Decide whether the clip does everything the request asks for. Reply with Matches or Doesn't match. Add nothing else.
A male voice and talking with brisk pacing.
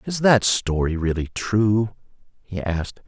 Doesn't match